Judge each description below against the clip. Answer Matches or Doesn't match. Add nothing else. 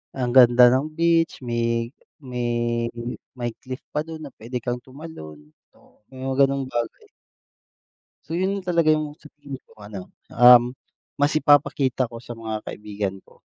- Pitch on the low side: Matches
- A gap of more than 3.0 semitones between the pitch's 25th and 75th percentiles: Matches